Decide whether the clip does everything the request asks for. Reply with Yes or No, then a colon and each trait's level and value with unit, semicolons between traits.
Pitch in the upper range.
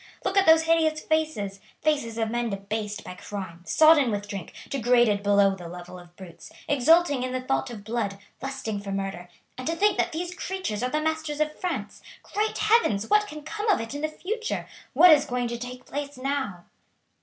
Yes: very high, 255 Hz